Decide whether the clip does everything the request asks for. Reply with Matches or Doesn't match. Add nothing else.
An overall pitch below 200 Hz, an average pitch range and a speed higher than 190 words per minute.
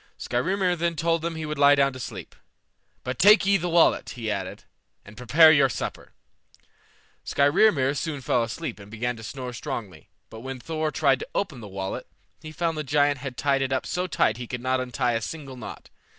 Matches